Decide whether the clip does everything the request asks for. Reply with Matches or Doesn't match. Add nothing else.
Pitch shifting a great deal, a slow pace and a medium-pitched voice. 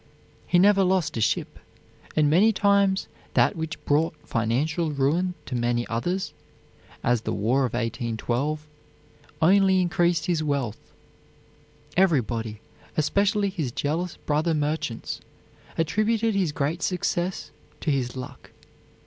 Matches